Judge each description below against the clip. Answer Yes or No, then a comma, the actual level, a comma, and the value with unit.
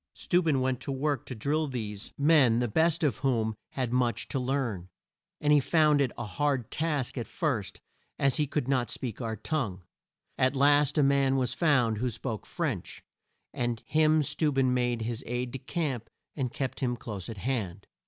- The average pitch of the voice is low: Yes, low, 130 Hz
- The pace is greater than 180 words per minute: Yes, average, 190 wpm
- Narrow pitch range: No, average, 3.6 semitones